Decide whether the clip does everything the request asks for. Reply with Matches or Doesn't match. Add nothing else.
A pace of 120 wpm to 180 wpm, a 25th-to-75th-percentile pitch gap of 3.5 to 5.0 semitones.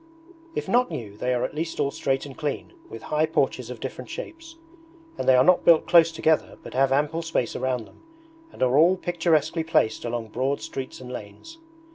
Doesn't match